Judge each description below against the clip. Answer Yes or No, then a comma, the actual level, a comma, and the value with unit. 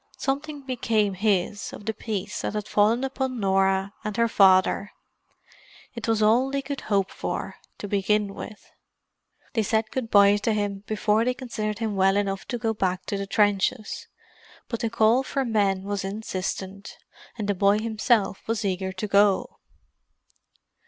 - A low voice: No, high, 210 Hz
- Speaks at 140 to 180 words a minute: Yes, average, 165 wpm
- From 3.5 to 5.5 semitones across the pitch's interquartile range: No, narrow, 2.5 semitones